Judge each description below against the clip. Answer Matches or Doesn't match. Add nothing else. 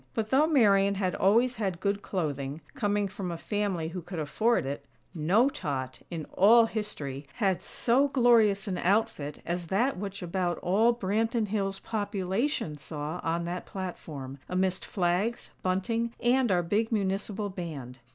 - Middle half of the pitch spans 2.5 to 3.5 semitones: Doesn't match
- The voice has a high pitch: Matches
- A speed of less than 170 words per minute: Matches